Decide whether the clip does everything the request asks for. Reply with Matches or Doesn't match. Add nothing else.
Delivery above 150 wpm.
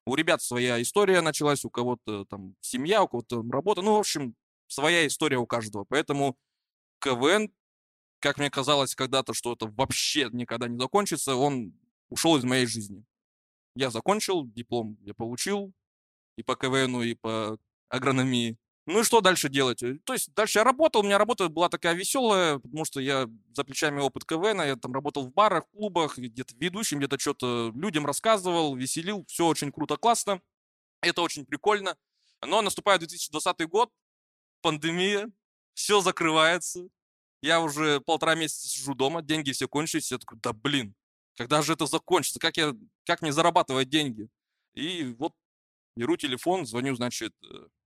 Matches